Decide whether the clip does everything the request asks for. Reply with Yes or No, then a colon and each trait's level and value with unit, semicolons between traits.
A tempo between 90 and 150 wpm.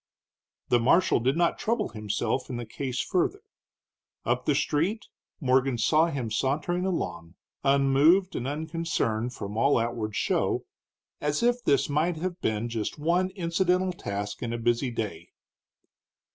Yes: average, 145 wpm